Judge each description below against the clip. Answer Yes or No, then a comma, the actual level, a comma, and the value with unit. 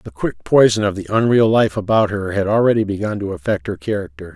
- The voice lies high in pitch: No, low, 105 Hz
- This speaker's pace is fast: Yes, fast, 220 wpm